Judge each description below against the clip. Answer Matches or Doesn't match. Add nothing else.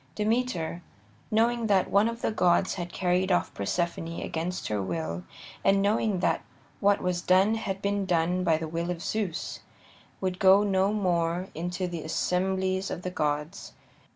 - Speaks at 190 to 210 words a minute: Doesn't match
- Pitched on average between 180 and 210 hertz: Matches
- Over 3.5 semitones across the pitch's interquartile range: Doesn't match